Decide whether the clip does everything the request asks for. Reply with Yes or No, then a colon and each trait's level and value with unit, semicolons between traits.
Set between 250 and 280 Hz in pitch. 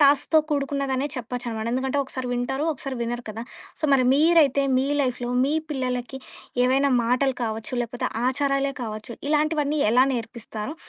Yes: very high, 260 Hz